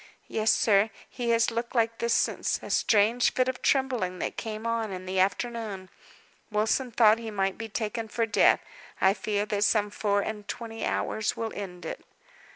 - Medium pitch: No, high, 220 Hz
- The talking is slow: No, average, 180 wpm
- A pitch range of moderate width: No, narrow, 2.2 semitones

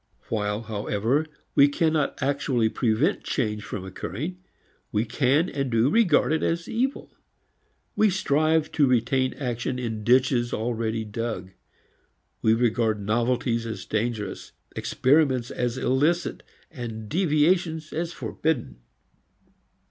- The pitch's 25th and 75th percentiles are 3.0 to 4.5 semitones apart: No, average, 5.3 semitones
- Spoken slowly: Yes, slow, 115 wpm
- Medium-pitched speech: No, low, 125 Hz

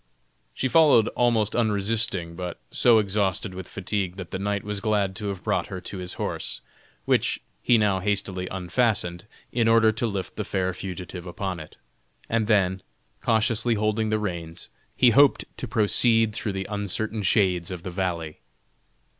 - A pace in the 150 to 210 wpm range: Yes, average, 165 wpm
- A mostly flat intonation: No, average, 3.2 semitones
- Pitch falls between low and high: No, low, 100 Hz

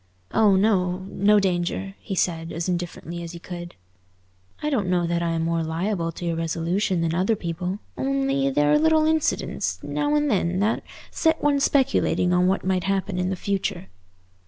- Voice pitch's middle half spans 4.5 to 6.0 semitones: No, average, 3.4 semitones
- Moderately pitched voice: Yes, medium, 180 Hz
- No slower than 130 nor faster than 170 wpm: No, average, 180 wpm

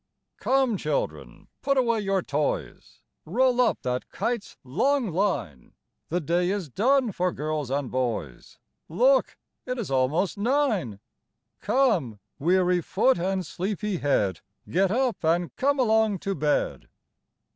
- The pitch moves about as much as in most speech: No, wide, 7.9 semitones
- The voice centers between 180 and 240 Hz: Yes, medium, 185 Hz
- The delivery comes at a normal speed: No, slow, 130 wpm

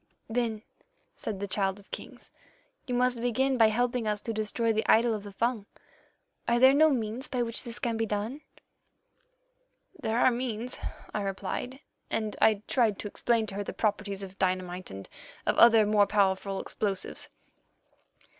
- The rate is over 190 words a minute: No, average, 165 wpm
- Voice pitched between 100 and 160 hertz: No, high, 220 Hz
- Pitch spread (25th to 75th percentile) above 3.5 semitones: No, average, 2.9 semitones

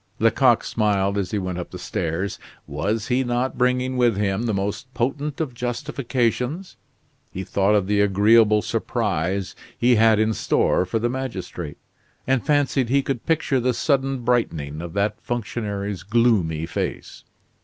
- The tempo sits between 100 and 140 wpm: No, average, 155 wpm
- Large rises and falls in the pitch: No, average, 4.2 semitones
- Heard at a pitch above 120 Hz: No, low, 115 Hz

